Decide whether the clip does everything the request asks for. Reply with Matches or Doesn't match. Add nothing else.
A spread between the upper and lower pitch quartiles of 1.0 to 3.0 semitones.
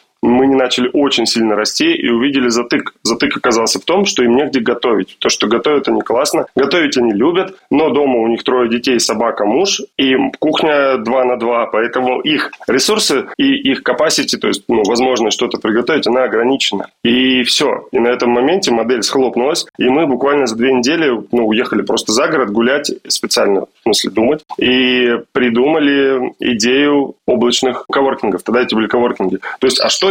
Matches